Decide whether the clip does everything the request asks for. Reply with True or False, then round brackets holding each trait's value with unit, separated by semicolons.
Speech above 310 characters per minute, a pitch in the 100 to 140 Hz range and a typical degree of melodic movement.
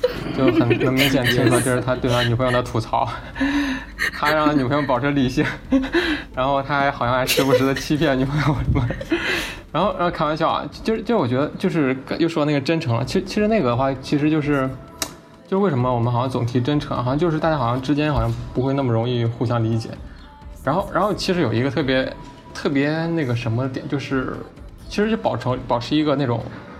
True (330 characters per minute; 135 Hz; 3.8 semitones)